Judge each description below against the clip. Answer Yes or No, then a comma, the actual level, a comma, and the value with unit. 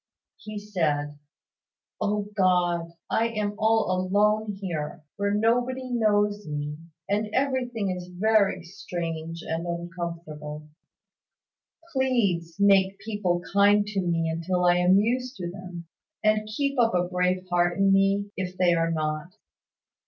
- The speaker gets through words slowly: Yes, slow, 130 wpm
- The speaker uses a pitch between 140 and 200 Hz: Yes, high, 190 Hz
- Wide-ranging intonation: No, average, 3.6 semitones